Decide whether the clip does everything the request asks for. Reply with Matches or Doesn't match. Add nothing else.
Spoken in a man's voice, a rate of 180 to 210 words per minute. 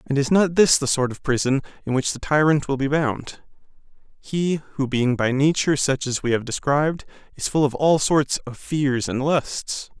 Matches